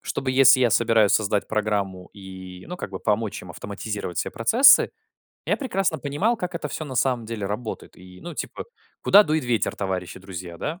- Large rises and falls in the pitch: Yes, wide, 7.0 semitones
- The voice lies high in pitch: No, low, 110 Hz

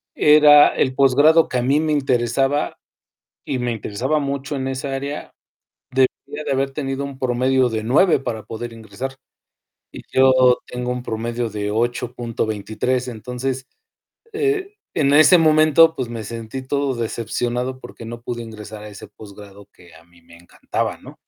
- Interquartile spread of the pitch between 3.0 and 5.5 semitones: Yes, average, 3.4 semitones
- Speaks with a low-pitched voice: Yes, low, 125 Hz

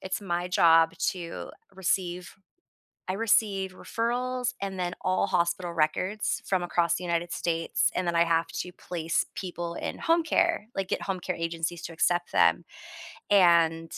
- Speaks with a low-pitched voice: No, medium, 175 Hz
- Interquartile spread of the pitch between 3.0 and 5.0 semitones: No, narrow, 2.4 semitones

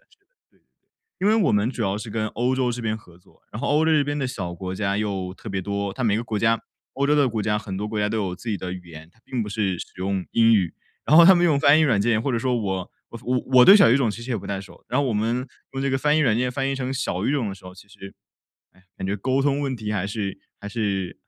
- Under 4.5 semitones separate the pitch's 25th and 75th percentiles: No, average, 4.8 semitones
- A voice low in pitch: Yes, low, 110 Hz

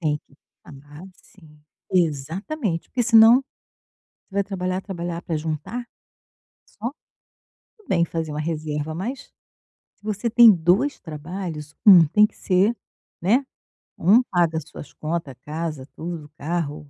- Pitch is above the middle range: No, medium, 170 Hz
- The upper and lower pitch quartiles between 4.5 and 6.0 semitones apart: Yes, average, 5.0 semitones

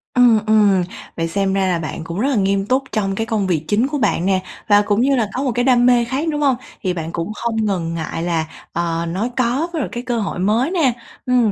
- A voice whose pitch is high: Yes, high, 210 Hz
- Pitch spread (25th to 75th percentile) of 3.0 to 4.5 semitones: No, average, 5.1 semitones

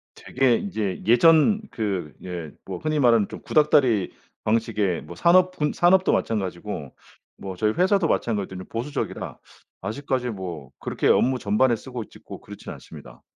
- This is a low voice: Yes, low, 115 Hz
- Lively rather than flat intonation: Yes, wide, 7.4 semitones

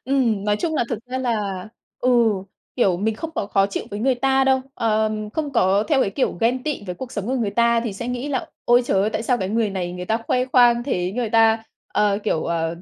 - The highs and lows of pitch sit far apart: No, average, 3.8 semitones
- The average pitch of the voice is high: Yes, high, 225 Hz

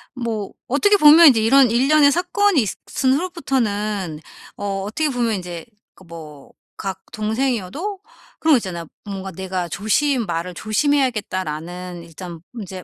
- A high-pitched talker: Yes, high, 215 Hz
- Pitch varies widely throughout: Yes, wide, 7.1 semitones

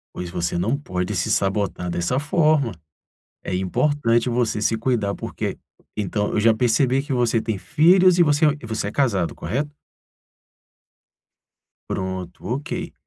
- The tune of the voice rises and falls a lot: Yes, wide, 6.3 semitones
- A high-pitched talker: No, low, 115 Hz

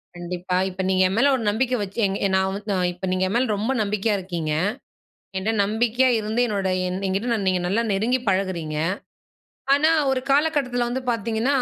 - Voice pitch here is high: Yes, high, 210 Hz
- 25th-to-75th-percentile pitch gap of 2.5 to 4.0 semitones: No, average, 4.4 semitones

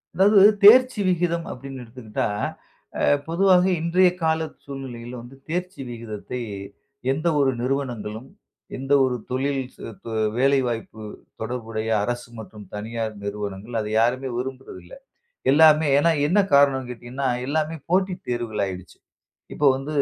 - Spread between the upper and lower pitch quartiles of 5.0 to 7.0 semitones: Yes, wide, 5.5 semitones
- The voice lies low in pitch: Yes, low, 130 Hz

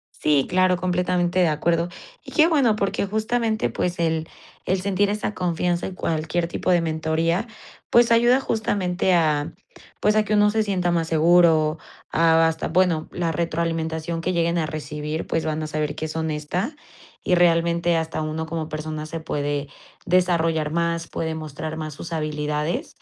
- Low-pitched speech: No, medium, 165 Hz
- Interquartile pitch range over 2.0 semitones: Yes, narrow, 2.5 semitones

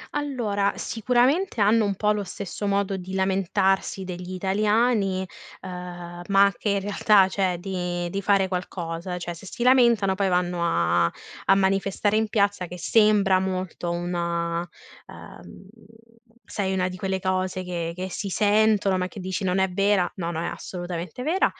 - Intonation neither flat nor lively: No, narrow, 2.2 semitones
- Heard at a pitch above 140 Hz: Yes, high, 190 Hz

